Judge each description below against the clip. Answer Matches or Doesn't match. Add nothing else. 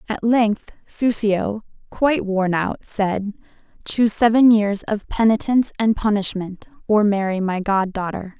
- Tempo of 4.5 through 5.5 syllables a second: Doesn't match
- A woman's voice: Matches